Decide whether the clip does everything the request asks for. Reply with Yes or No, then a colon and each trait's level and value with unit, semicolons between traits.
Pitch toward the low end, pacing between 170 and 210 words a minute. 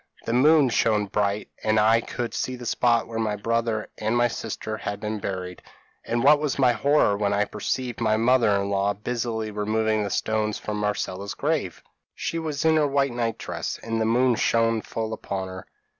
Yes: low, 110 Hz; average, 195 wpm